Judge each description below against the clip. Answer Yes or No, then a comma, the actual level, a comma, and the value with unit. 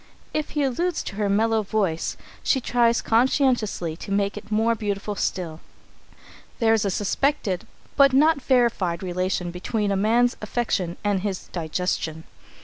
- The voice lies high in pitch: Yes, high, 210 Hz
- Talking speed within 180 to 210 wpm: No, average, 145 wpm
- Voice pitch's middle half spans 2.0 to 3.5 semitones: No, average, 4.4 semitones